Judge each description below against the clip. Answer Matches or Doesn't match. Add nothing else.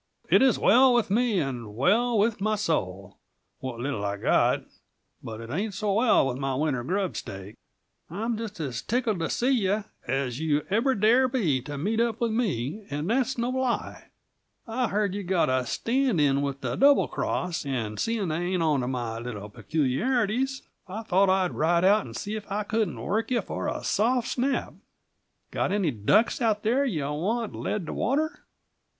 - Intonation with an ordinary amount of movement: Doesn't match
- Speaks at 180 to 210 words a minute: Matches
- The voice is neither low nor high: Doesn't match